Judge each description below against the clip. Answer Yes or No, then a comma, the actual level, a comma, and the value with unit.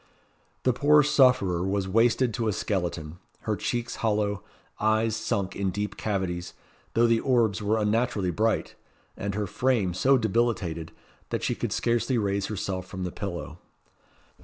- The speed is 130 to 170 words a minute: Yes, average, 150 wpm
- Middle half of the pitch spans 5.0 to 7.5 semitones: No, average, 3.6 semitones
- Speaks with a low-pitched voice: Yes, low, 105 Hz